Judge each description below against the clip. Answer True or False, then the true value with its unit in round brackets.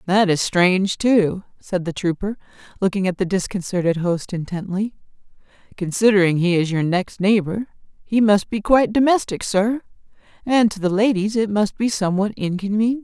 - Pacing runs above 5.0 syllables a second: True (5.2 syllables/s)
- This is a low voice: False (200 Hz)